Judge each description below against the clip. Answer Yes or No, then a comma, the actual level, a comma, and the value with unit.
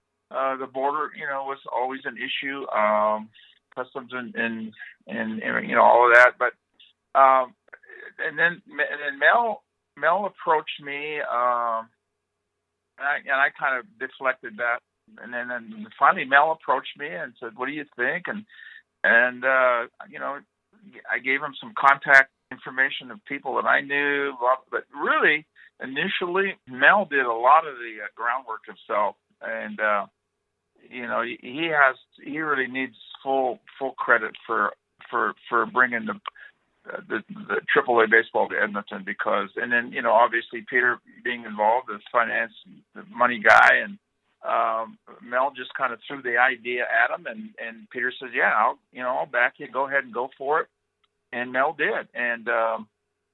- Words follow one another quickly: No, average, 170 wpm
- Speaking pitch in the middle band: No, low, 130 Hz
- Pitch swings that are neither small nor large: Yes, average, 3.7 semitones